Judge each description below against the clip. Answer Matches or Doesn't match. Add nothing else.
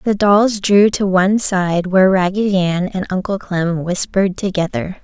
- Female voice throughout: Matches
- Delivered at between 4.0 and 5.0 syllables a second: Matches